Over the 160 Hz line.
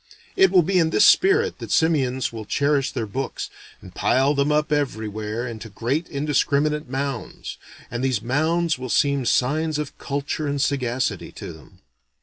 No: medium, 140 Hz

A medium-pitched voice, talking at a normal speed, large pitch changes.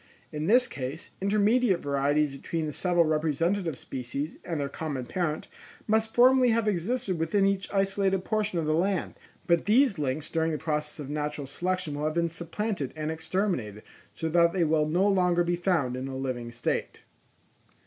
No: medium, 165 Hz; average, 175 wpm; average, 4.6 semitones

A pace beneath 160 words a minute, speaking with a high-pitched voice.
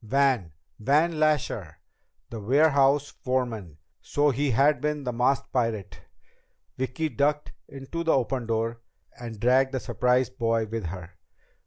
No: slow, 135 wpm; low, 130 Hz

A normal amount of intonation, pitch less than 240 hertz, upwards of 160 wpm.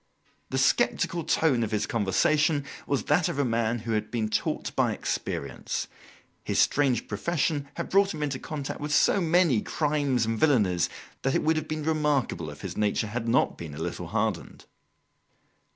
No: wide, 5.9 semitones; low, 135 Hz; average, 175 wpm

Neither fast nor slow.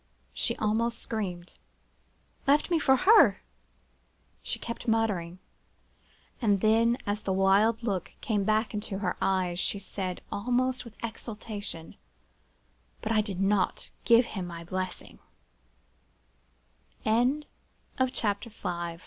No: slow, 105 wpm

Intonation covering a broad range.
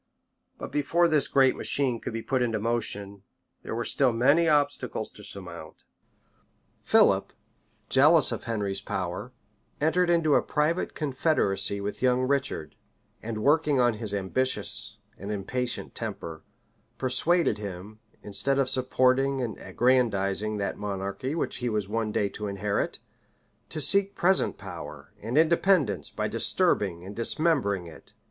Yes: wide, 5.8 semitones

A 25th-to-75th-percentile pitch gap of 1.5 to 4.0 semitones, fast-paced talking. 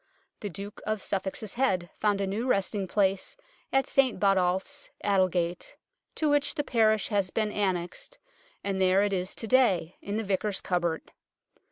No: average, 2.7 semitones; average, 160 wpm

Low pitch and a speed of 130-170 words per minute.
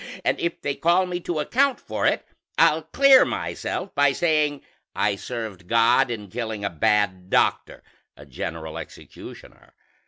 Yes: low, 120 Hz; average, 150 wpm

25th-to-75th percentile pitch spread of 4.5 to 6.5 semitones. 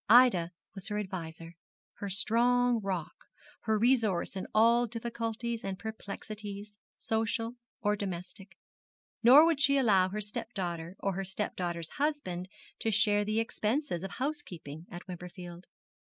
No: average, 4.0 semitones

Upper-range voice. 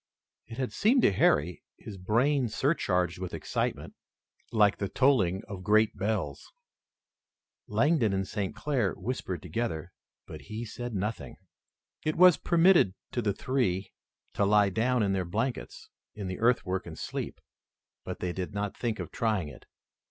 No: low, 105 Hz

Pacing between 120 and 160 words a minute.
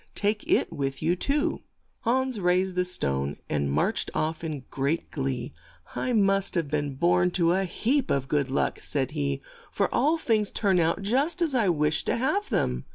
No: fast, 205 wpm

